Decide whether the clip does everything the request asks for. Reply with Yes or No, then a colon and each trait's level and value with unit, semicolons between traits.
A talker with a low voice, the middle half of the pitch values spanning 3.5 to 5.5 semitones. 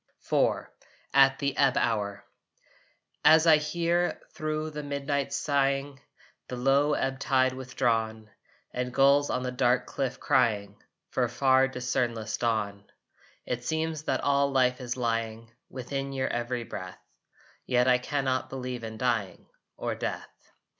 No: low, 130 Hz; average, 2.8 semitones